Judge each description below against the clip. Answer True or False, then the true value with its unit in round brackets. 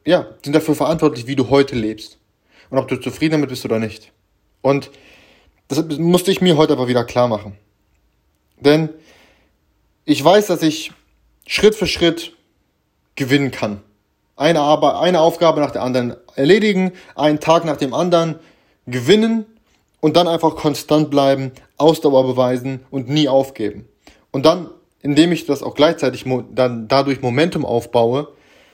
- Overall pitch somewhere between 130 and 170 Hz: True (140 Hz)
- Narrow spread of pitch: False (4.4 semitones)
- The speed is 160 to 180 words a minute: False (150 wpm)